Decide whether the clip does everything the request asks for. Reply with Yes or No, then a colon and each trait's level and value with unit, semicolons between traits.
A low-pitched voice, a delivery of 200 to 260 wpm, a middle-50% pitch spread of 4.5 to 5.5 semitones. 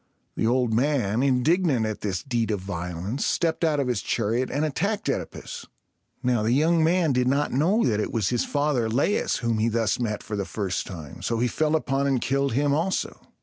Yes: low, 125 Hz; fast, 205 wpm; average, 4.9 semitones